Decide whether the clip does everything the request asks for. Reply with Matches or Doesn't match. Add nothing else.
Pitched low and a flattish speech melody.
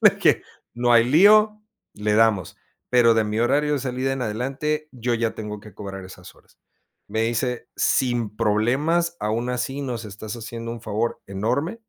Doesn't match